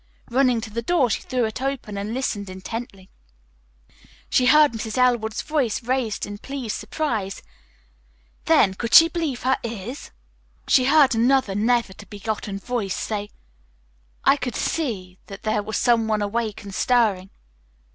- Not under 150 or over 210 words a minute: Yes, average, 155 wpm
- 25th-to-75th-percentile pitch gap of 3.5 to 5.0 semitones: Yes, average, 3.8 semitones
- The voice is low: No, high, 230 Hz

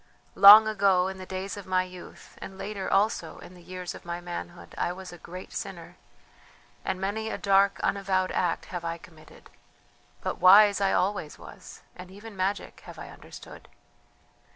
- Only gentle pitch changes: Yes, narrow, 1.8 semitones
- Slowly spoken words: No, average, 175 wpm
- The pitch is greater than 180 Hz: Yes, high, 190 Hz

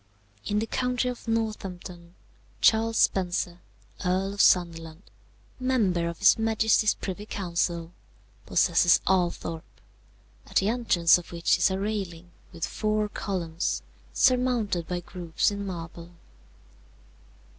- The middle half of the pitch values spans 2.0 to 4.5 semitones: Yes, average, 3.8 semitones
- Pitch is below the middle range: No, high, 190 Hz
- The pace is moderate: No, slow, 115 wpm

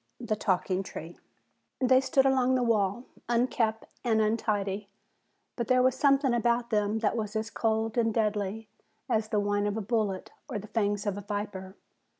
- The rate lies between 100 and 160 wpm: No, average, 170 wpm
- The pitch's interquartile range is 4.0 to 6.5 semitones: No, average, 2.7 semitones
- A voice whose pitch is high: Yes, high, 220 Hz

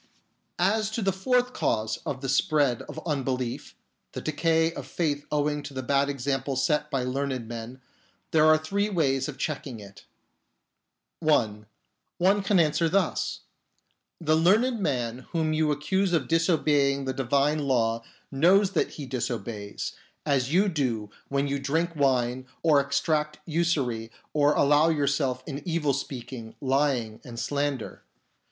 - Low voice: No, medium, 145 Hz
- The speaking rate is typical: Yes, average, 150 wpm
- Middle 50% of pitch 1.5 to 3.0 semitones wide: No, average, 3.9 semitones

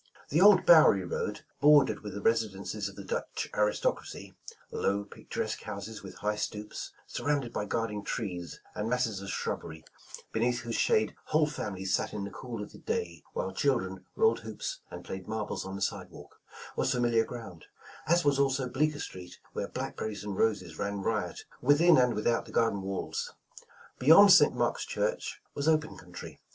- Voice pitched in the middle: No, low, 110 Hz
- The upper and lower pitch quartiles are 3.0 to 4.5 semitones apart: No, wide, 5.6 semitones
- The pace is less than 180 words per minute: No, average, 185 wpm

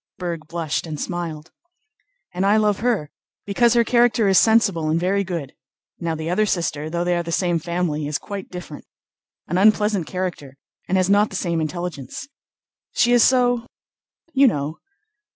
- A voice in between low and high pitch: Yes, medium, 180 Hz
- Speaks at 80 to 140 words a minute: No, average, 165 wpm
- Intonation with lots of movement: No, average, 4.4 semitones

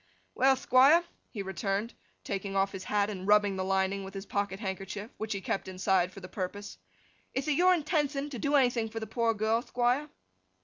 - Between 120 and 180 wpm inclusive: No, average, 195 wpm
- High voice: Yes, high, 210 Hz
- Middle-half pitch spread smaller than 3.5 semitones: No, average, 4.7 semitones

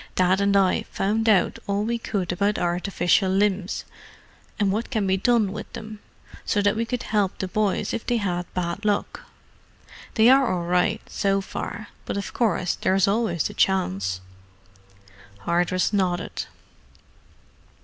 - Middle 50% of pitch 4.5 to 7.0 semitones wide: No, average, 2.8 semitones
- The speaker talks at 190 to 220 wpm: No, average, 155 wpm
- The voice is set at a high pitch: Yes, high, 200 Hz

